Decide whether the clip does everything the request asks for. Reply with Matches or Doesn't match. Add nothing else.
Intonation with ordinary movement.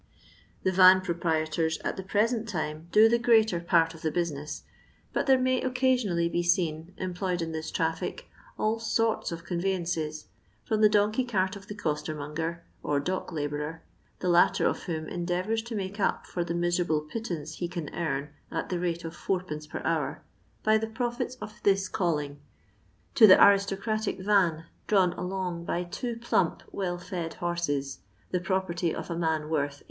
Matches